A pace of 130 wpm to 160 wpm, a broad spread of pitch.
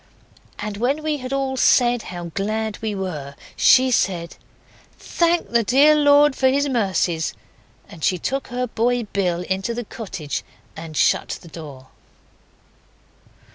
Yes: average, 140 wpm; wide, 6.7 semitones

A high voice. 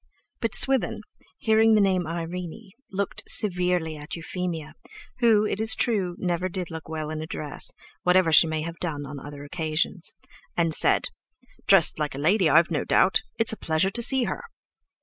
No: medium, 175 Hz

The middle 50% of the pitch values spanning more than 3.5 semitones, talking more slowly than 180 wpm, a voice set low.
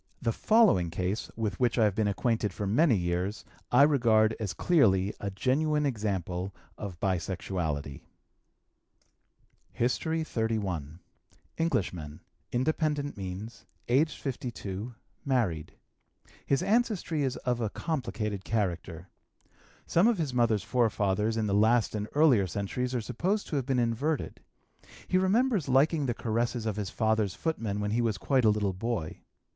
Yes: wide, 5.5 semitones; average, 140 wpm; low, 115 Hz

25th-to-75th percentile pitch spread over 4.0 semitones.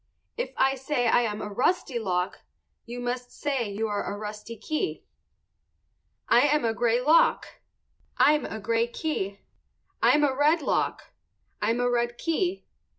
Yes: average, 5.0 semitones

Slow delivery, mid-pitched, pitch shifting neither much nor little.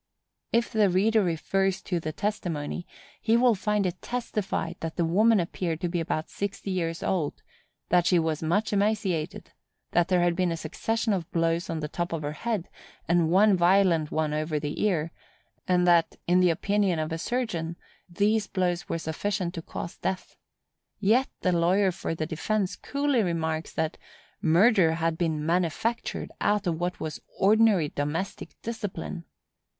No: average, 165 wpm; medium, 175 Hz; average, 3.8 semitones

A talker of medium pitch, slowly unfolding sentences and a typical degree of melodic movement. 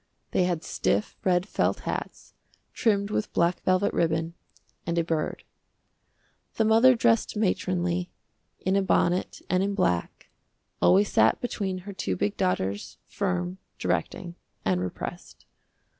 Yes: medium, 180 Hz; slow, 130 wpm; average, 3.8 semitones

